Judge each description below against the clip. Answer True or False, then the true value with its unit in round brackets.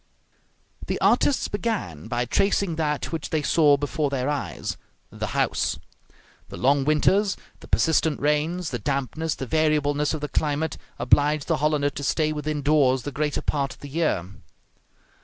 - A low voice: False (150 Hz)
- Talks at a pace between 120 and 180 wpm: True (160 wpm)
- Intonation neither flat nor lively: False (1.9 semitones)